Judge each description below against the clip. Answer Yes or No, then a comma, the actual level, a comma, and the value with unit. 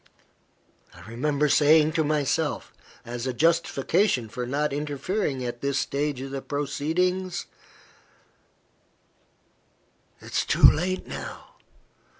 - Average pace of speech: No, slow, 110 wpm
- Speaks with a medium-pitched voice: Yes, medium, 145 Hz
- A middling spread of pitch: Yes, average, 3.2 semitones